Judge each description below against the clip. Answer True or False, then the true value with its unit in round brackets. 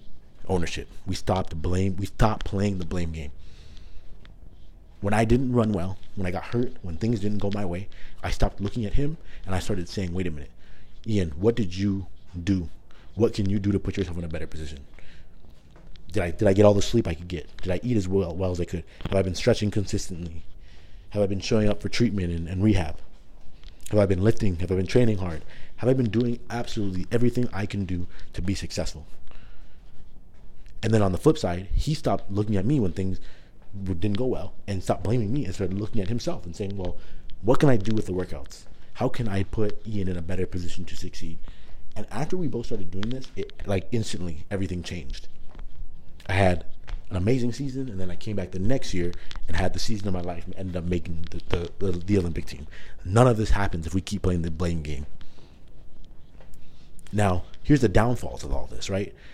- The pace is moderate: False (220 wpm)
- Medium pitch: False (95 Hz)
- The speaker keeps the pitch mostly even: False (3.6 semitones)